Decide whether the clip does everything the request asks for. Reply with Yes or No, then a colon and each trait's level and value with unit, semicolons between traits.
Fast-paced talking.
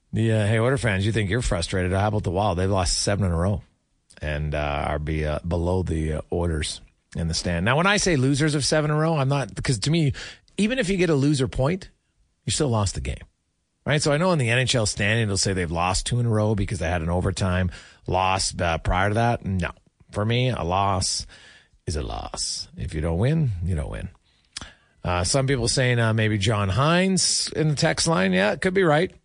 Yes: fast, 230 wpm